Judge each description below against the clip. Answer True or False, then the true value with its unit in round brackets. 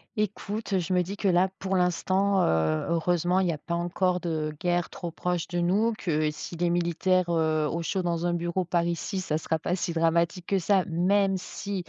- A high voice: False (175 Hz)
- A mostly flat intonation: True (2.0 semitones)